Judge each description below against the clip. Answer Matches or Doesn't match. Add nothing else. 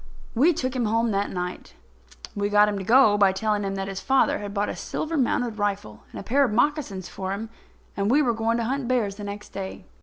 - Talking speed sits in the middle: Doesn't match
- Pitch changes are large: Doesn't match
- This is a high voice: Matches